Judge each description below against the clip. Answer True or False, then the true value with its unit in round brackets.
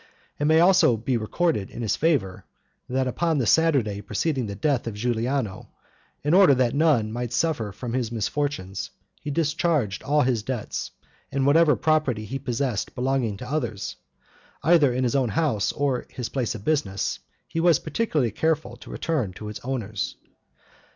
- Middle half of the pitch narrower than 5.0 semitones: False (5.6 semitones)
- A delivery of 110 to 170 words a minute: True (165 wpm)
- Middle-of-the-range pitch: False (130 Hz)